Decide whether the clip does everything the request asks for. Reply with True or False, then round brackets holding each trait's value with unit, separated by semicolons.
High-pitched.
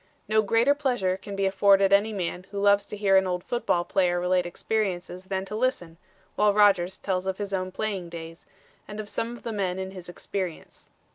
True (195 Hz)